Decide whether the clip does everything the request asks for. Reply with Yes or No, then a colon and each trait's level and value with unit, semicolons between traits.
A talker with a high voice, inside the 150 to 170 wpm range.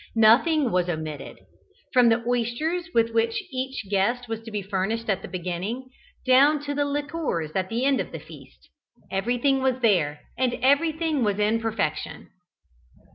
Yes: high, 230 Hz; average, 160 wpm